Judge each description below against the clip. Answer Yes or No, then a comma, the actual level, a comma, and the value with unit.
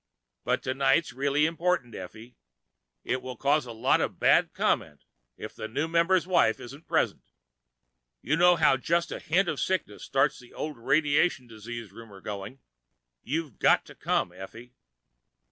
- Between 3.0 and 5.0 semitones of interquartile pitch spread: No, wide, 5.6 semitones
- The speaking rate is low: No, average, 155 wpm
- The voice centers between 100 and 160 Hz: Yes, low, 135 Hz